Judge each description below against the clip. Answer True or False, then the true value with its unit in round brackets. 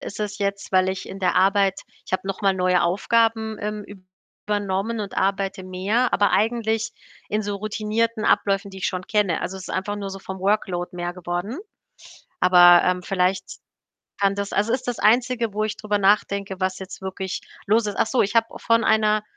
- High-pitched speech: True (200 Hz)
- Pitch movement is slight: True (2.2 semitones)